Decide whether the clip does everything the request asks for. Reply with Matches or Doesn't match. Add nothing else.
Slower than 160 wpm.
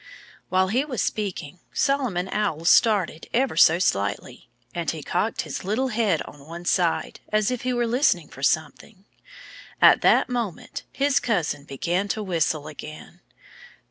Matches